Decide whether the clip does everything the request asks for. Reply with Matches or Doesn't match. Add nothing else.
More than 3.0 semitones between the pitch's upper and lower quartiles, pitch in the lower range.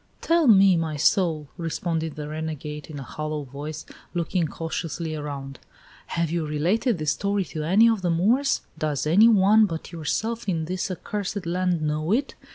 Doesn't match